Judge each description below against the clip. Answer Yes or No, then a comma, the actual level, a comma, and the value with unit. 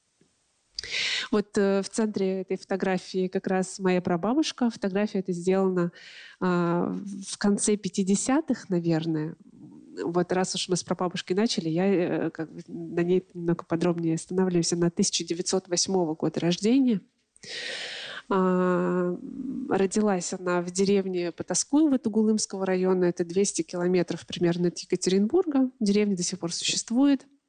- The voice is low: No, medium, 185 Hz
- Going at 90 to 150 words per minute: Yes, slow, 110 wpm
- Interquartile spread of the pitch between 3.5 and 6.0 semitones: No, average, 2.9 semitones